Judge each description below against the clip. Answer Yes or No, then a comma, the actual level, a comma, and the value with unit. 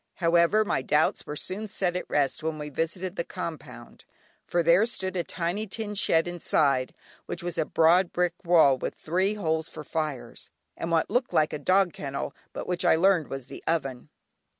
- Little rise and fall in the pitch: No, average, 3.3 semitones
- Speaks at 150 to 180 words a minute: No, average, 190 wpm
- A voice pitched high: No, medium, 170 Hz